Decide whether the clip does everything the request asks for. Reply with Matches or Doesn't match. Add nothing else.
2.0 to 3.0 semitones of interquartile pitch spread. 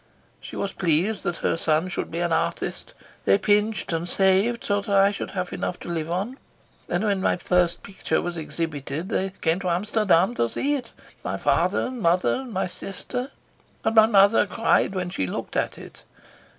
Doesn't match